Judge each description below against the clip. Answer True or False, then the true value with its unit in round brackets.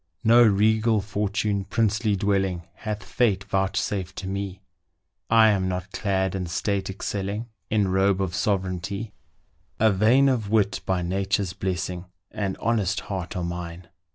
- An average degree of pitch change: False (2.1 semitones)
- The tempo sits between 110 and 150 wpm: True (140 wpm)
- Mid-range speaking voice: False (100 Hz)